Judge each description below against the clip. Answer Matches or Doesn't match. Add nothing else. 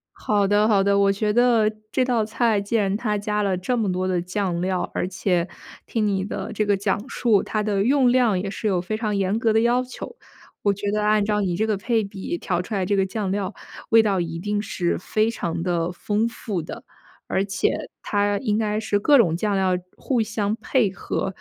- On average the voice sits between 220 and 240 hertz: Doesn't match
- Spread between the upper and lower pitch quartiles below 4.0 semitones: Matches